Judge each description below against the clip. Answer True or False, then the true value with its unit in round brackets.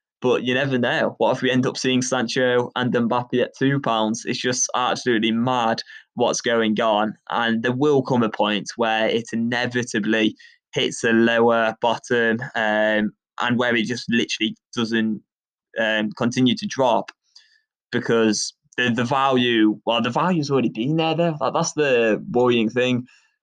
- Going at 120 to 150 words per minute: False (160 wpm)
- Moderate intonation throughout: False (2.3 semitones)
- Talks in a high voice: False (120 Hz)